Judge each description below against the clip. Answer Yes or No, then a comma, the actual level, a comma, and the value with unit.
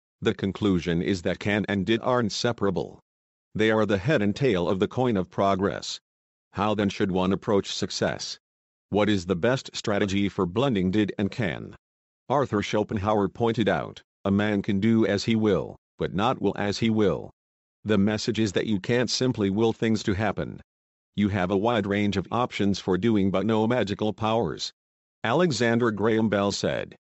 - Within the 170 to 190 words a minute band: Yes, average, 180 wpm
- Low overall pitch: Yes, low, 105 Hz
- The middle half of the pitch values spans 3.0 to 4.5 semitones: No, narrow, 2.5 semitones